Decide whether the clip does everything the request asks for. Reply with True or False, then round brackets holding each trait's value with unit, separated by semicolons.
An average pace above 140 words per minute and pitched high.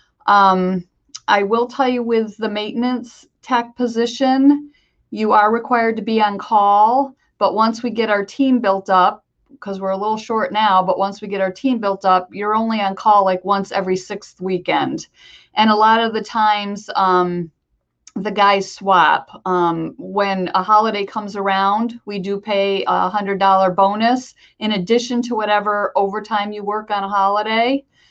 True (170 wpm; 210 Hz)